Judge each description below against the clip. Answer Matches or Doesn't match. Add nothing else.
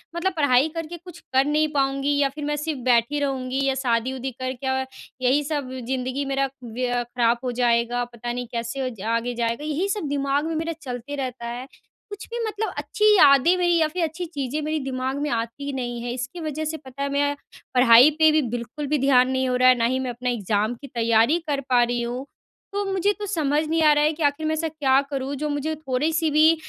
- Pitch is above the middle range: Matches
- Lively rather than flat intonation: Doesn't match